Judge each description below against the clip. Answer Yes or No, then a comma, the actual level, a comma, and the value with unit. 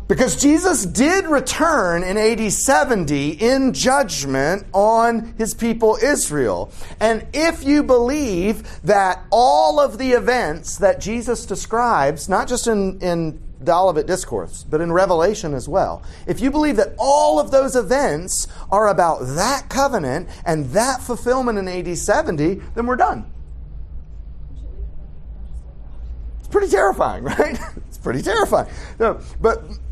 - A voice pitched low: No, high, 215 Hz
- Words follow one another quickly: No, slow, 135 wpm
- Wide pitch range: Yes, wide, 8.5 semitones